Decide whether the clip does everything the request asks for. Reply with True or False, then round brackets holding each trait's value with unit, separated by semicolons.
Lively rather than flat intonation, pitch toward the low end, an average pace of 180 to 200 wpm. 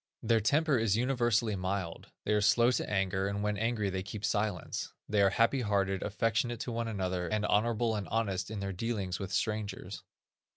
False (2.8 semitones; 105 Hz; 190 wpm)